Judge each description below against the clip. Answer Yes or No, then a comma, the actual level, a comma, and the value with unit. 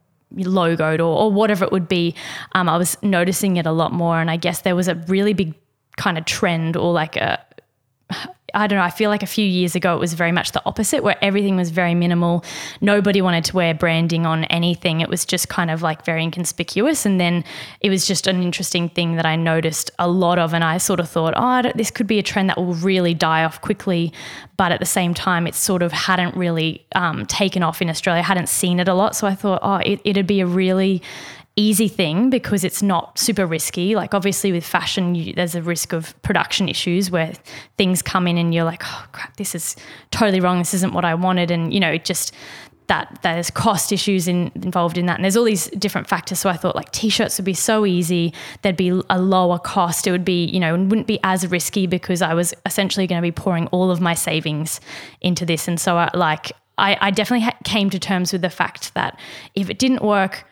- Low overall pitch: No, medium, 180 Hz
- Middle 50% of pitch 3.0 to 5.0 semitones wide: No, narrow, 2.5 semitones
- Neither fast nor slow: No, fast, 235 wpm